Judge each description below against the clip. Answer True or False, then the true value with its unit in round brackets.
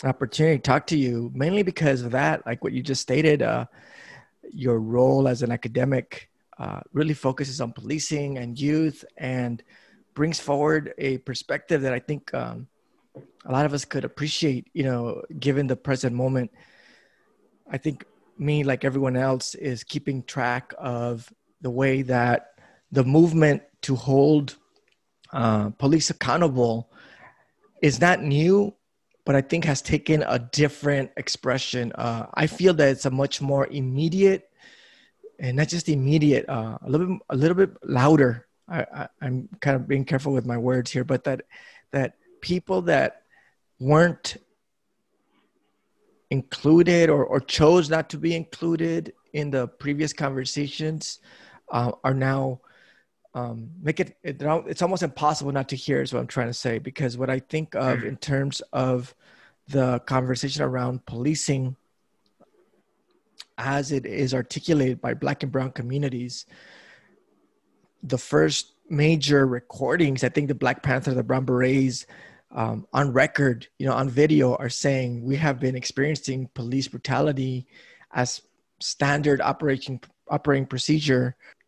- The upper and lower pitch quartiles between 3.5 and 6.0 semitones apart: False (2.9 semitones)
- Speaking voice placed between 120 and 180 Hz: True (135 Hz)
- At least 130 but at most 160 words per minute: True (150 wpm)